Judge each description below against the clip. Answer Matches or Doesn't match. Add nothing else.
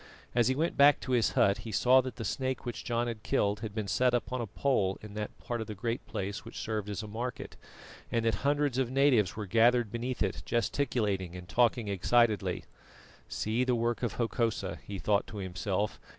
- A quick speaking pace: Matches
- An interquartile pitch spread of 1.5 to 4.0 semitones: Matches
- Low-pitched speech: Matches